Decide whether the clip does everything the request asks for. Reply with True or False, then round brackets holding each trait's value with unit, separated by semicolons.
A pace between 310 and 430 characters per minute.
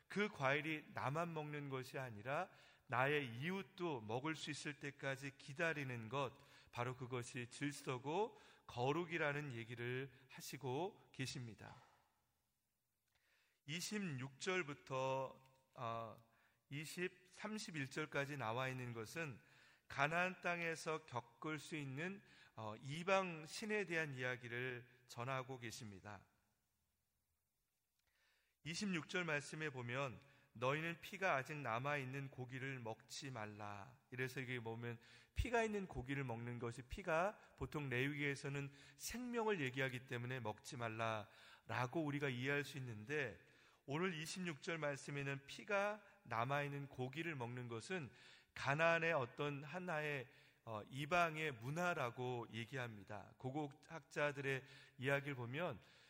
False (240 characters per minute)